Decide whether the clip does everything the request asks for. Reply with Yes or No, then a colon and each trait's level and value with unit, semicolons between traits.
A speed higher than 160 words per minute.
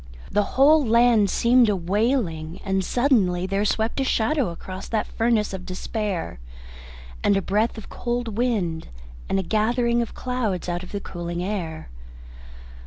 No: average, 155 wpm